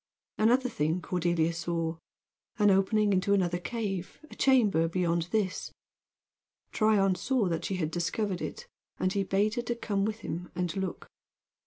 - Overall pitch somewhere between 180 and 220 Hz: Yes, high, 190 Hz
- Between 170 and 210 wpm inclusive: No, average, 155 wpm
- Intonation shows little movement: No, average, 3.7 semitones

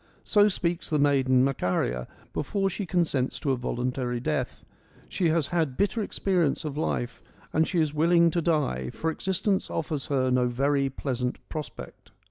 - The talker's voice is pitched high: No, medium, 150 Hz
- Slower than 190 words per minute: Yes, average, 160 wpm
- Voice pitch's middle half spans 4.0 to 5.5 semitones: Yes, average, 4.9 semitones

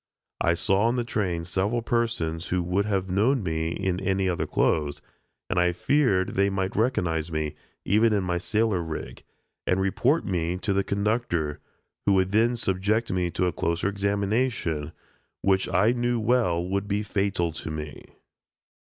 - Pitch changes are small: No, average, 3.7 semitones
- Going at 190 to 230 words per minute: No, average, 165 wpm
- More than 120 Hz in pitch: No, very low, 95 Hz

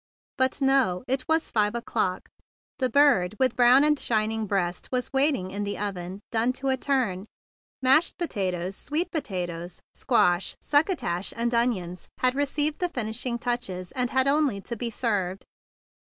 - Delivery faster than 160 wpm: No, average, 155 wpm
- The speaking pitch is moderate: No, high, 235 Hz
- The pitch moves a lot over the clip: Yes, wide, 5.8 semitones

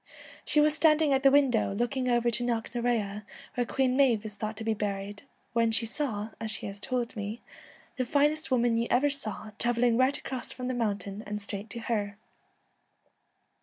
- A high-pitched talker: Yes, high, 235 Hz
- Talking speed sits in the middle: Yes, average, 190 wpm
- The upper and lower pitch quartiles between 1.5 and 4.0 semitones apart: Yes, average, 3.3 semitones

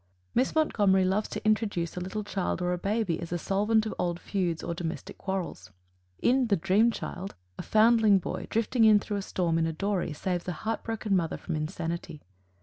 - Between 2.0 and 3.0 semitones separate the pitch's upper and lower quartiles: No, average, 3.8 semitones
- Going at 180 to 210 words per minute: Yes, average, 200 wpm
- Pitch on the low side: No, high, 195 Hz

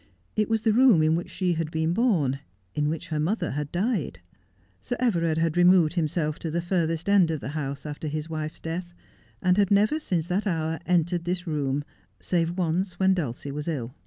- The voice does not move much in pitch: No, average, 3.1 semitones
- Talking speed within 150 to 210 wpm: Yes, fast, 205 wpm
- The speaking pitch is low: No, medium, 165 Hz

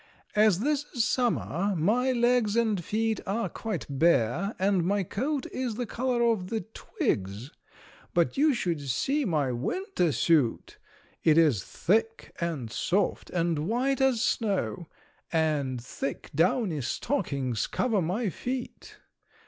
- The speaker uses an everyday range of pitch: No, wide, 7.0 semitones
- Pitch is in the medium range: No, high, 195 Hz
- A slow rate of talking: Yes, slow, 130 wpm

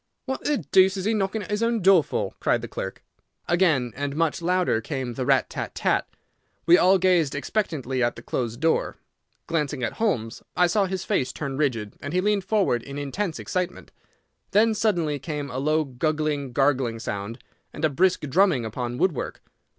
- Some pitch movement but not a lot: No, wide, 6.2 semitones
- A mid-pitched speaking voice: Yes, medium, 155 Hz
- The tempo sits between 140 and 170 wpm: No, average, 185 wpm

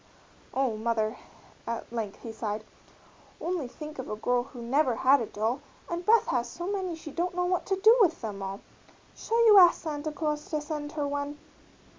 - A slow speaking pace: No, average, 195 wpm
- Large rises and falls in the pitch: Yes, wide, 6.7 semitones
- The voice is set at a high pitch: Yes, very high, 290 Hz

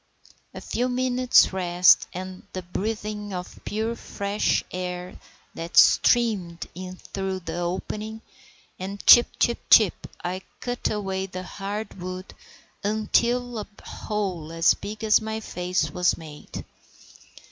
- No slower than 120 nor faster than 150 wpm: Yes, slow, 135 wpm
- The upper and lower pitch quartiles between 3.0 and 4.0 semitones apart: Yes, average, 3.3 semitones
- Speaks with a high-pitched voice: Yes, high, 195 Hz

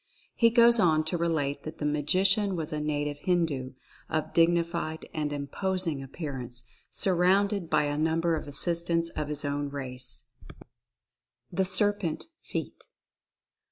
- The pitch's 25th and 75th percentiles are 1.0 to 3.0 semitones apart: No, average, 3.4 semitones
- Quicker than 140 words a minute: No, slow, 135 wpm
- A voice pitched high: No, medium, 160 Hz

